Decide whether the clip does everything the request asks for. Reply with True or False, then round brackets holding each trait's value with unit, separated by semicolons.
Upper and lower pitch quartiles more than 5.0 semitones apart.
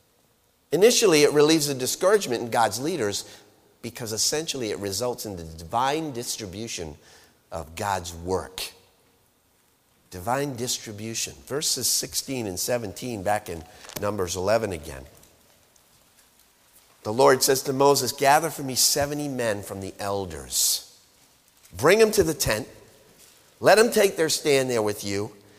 True (5.4 semitones)